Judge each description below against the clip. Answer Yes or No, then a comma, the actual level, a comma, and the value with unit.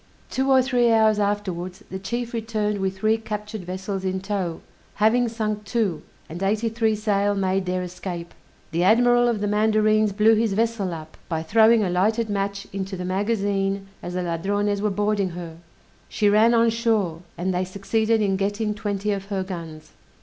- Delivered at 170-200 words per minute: Yes, average, 180 wpm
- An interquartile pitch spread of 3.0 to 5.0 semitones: No, narrow, 2.6 semitones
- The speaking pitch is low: No, high, 205 Hz